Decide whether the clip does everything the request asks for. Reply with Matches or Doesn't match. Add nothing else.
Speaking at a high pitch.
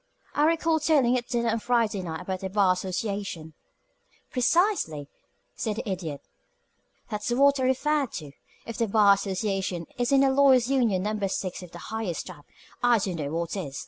Matches